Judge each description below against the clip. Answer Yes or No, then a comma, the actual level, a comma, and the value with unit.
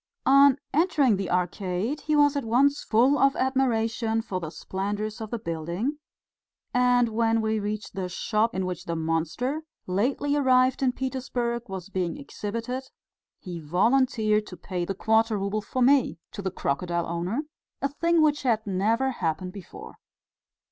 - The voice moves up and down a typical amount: No, wide, 5.7 semitones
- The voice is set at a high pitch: Yes, high, 225 Hz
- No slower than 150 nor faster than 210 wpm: Yes, average, 155 wpm